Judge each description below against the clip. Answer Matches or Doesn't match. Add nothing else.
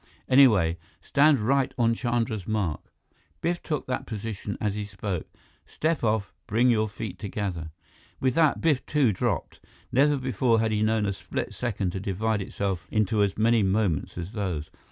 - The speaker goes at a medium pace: Matches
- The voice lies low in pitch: Matches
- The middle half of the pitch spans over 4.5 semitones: Doesn't match